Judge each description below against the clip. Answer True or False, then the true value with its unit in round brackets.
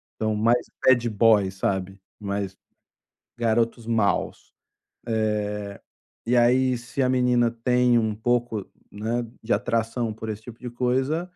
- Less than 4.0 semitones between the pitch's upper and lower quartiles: True (2.4 semitones)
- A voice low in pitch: True (115 Hz)